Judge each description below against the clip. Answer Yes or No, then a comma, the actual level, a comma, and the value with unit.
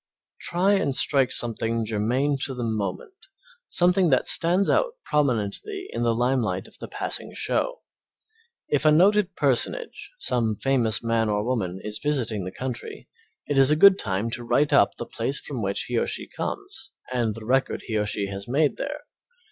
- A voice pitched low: Yes, low, 130 Hz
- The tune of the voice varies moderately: No, wide, 6.3 semitones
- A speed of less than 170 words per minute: No, average, 180 wpm